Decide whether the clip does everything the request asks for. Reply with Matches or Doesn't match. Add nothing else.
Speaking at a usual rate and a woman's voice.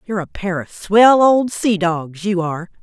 Doesn't match